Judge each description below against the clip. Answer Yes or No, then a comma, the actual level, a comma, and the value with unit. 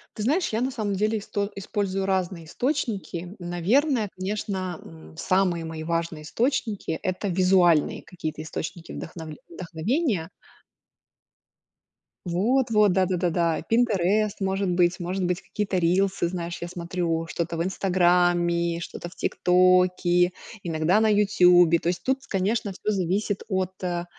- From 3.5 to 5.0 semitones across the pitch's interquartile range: No, average, 3.0 semitones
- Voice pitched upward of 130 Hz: Yes, medium, 185 Hz